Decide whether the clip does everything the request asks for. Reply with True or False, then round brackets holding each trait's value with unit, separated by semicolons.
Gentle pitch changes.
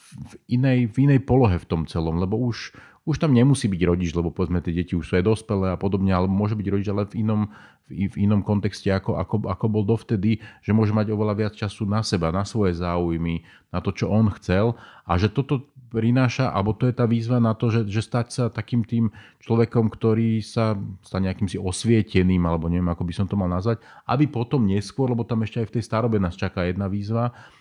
False (3.6 semitones)